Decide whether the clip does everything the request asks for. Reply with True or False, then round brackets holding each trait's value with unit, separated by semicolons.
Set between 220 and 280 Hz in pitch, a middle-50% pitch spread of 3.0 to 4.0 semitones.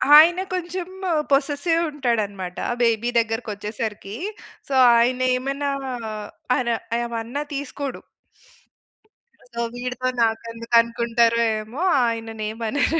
True (235 Hz; 3.6 semitones)